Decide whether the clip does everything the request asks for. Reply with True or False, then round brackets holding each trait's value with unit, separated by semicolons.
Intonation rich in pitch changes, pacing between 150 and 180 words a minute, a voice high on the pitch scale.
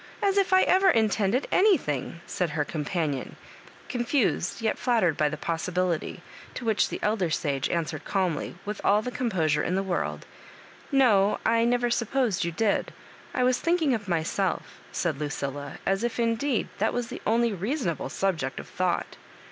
True (6.2 semitones; 170 wpm; 200 Hz)